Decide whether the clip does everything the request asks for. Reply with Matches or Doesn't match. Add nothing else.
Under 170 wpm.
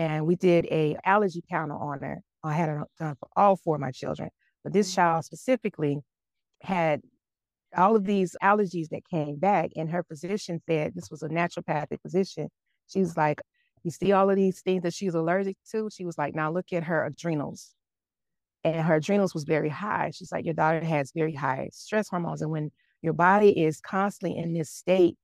Doesn't match